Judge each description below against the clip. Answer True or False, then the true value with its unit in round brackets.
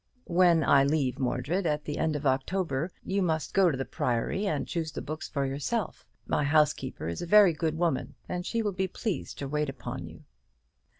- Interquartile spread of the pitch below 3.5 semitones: False (4.5 semitones)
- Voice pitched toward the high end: False (155 Hz)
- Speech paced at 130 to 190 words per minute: False (200 wpm)